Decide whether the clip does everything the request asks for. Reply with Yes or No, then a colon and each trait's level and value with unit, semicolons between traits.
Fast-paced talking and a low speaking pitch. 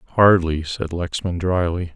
No: slow, 125 wpm; very low, 85 Hz